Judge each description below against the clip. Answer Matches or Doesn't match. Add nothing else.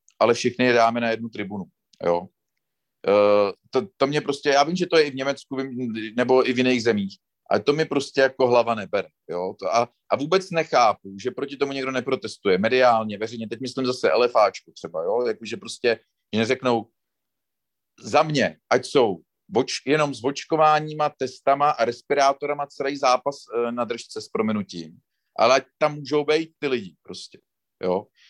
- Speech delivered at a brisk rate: Matches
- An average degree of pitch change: Matches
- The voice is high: Doesn't match